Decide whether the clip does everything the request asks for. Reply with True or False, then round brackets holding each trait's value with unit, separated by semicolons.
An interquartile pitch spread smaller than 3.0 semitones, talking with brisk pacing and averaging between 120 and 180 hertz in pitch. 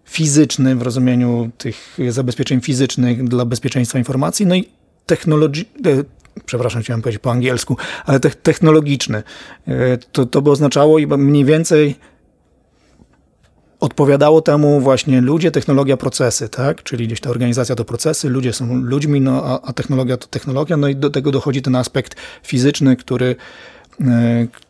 False (2.6 semitones; 135 wpm; 135 Hz)